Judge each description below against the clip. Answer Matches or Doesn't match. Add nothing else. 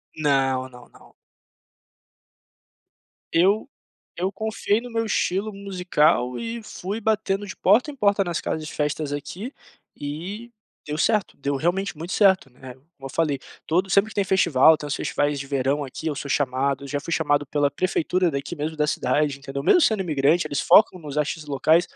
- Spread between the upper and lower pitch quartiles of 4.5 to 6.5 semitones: Matches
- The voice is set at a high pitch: Doesn't match